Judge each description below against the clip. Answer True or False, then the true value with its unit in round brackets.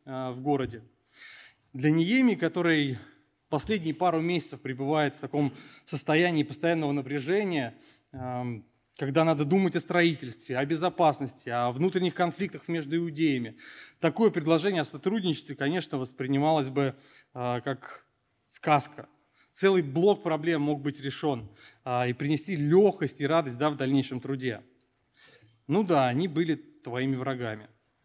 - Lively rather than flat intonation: False (4.2 semitones)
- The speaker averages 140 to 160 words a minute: False (120 wpm)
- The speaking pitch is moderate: True (145 Hz)